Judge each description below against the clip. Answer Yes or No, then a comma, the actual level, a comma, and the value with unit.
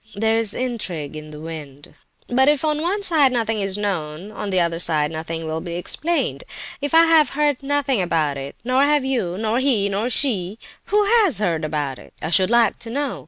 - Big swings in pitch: Yes, wide, 8.9 semitones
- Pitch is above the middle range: Yes, high, 215 Hz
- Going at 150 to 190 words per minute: No, fast, 205 wpm